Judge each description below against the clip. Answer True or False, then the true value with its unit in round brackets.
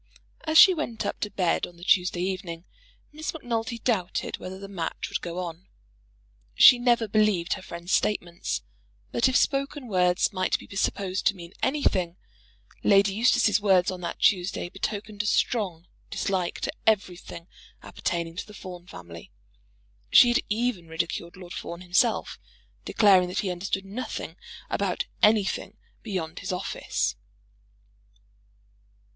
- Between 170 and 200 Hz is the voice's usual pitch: True (190 Hz)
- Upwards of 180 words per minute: False (140 wpm)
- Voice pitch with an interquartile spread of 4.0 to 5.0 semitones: False (3.6 semitones)